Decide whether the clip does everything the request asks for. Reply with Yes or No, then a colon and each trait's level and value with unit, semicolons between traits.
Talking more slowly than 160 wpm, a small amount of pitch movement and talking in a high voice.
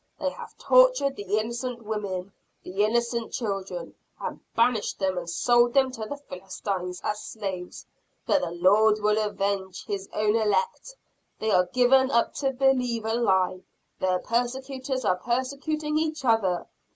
No: average, 150 wpm; average, 4.9 semitones; high, 220 Hz